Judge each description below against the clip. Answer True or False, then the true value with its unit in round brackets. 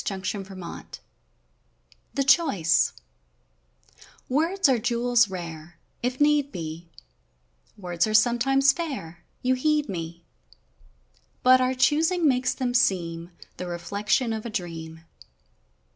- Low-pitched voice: False (220 Hz)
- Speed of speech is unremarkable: False (115 wpm)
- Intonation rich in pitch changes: True (7.3 semitones)